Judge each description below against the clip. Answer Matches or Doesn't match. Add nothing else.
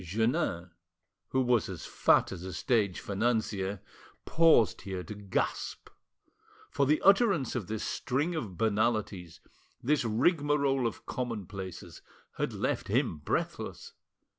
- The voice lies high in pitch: Doesn't match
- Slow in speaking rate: Matches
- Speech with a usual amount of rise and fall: Doesn't match